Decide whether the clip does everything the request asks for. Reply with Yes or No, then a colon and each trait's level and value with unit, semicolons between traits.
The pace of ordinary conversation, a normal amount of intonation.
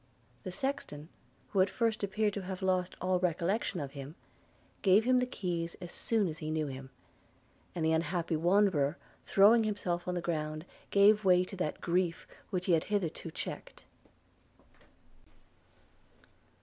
Yes: average, 155 wpm; average, 3.6 semitones